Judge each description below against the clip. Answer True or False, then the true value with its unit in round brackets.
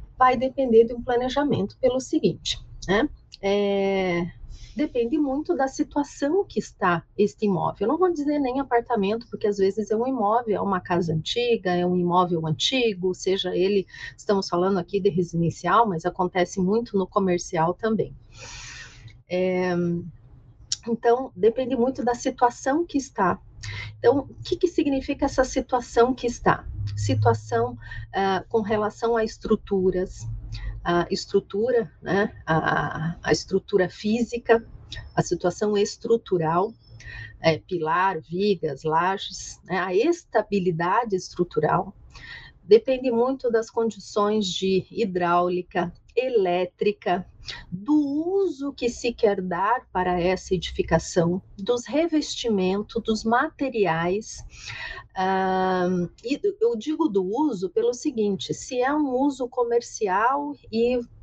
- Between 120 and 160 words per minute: True (125 wpm)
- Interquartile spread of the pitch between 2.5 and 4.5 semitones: False (5.5 semitones)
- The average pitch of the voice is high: True (205 Hz)